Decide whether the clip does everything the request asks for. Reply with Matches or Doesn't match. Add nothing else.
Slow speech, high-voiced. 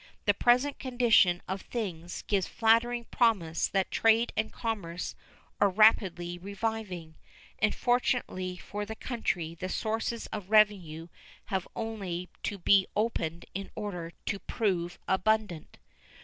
Matches